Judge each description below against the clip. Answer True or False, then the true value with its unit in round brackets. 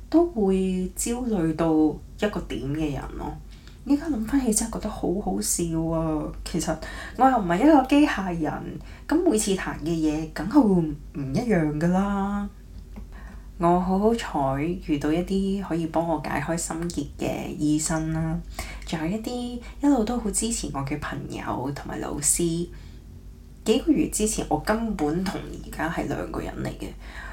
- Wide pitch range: True (5.7 semitones)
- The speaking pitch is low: False (175 Hz)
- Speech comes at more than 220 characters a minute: True (230 characters per minute)